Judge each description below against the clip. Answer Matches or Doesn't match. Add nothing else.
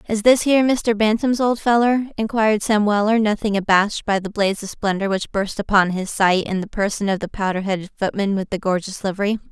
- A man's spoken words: Doesn't match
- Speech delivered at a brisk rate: Matches